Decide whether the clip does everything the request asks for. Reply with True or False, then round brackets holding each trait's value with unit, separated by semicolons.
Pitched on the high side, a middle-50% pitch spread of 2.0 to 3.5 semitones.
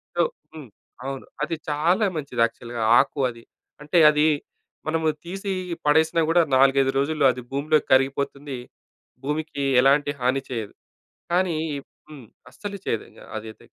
False (145 Hz; 3.2 semitones)